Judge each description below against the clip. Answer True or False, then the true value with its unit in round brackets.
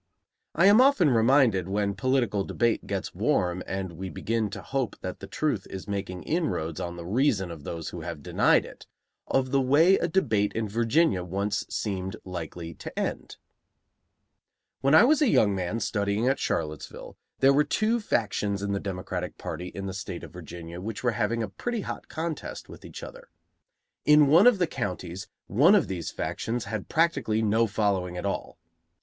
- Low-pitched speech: True (105 Hz)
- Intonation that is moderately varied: False (6.8 semitones)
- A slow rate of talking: False (180 wpm)